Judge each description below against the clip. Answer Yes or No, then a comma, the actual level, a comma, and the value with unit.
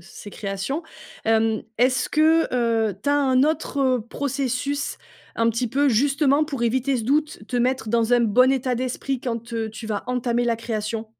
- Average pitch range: Yes, average, 3.2 semitones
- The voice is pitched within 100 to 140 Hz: No, high, 245 Hz